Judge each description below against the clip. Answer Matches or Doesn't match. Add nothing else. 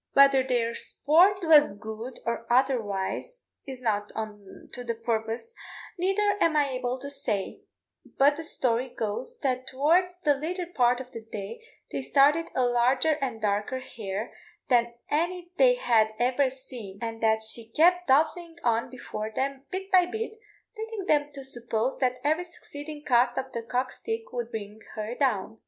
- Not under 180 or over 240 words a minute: Doesn't match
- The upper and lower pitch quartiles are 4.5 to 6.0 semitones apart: Matches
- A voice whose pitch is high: Matches